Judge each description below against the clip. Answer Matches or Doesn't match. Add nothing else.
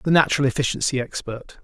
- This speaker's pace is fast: Doesn't match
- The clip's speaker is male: Matches